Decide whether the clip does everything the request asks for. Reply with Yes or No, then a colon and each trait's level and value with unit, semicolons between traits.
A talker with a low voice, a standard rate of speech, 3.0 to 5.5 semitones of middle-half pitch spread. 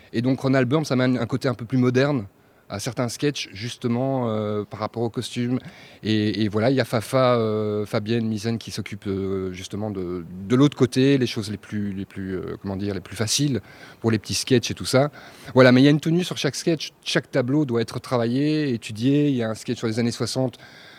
No: low, 120 Hz; fast, 235 wpm; average, 3.7 semitones